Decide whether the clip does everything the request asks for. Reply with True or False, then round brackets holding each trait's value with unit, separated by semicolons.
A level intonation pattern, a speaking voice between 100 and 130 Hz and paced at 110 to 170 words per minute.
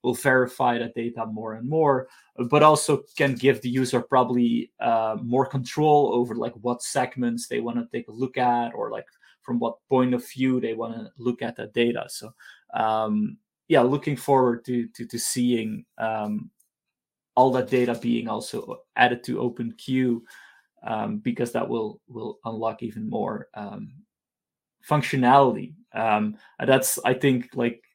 True (2.0 semitones; 125 Hz; 165 wpm)